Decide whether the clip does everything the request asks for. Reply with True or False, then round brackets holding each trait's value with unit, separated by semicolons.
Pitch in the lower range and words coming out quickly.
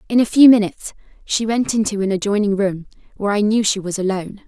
False (205 Hz; 215 wpm)